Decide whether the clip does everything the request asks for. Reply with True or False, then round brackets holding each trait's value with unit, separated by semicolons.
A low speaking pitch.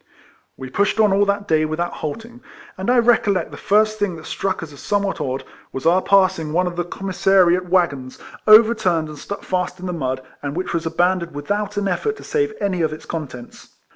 False (185 Hz)